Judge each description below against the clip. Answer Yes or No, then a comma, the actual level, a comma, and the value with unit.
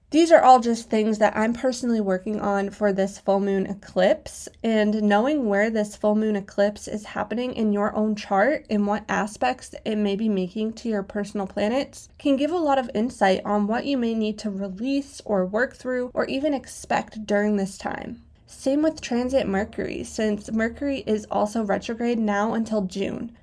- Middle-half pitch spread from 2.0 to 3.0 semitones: No, average, 3.4 semitones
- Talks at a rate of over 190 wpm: No, average, 185 wpm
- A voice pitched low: No, high, 215 Hz